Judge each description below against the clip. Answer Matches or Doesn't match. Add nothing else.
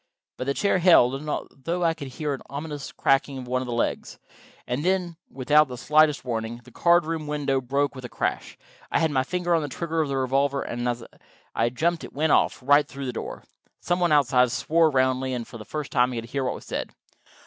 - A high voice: Doesn't match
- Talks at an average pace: Doesn't match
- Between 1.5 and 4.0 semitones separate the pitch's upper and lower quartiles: Matches